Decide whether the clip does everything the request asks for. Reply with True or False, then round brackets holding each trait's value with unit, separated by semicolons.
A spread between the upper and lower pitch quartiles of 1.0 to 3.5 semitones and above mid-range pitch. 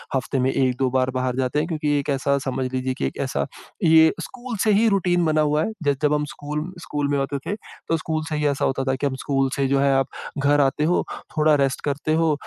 False (2.8 semitones; 145 Hz)